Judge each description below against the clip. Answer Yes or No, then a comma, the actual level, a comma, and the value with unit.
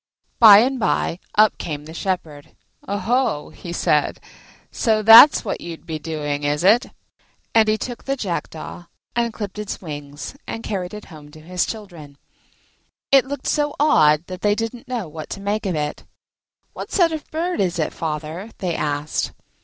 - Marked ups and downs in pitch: Yes, wide, 6.5 semitones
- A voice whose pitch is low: No, high, 190 Hz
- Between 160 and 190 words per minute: Yes, average, 170 wpm